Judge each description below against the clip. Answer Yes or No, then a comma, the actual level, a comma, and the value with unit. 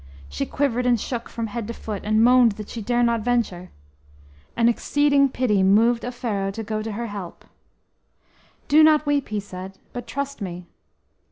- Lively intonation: No, average, 3.3 semitones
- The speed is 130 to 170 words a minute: No, average, 180 wpm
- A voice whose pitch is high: Yes, high, 230 Hz